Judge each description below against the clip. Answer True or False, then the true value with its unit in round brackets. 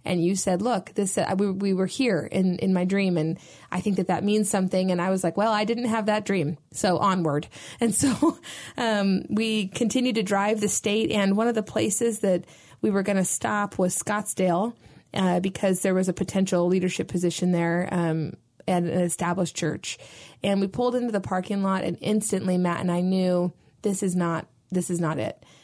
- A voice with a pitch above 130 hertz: True (190 Hz)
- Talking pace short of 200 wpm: False (205 wpm)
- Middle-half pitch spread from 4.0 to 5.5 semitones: False (2.8 semitones)